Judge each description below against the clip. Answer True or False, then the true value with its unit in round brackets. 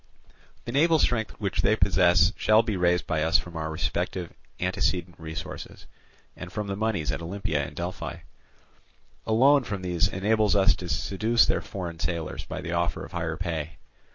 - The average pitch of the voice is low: True (90 Hz)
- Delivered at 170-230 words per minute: True (175 wpm)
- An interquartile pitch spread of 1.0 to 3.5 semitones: False (4.1 semitones)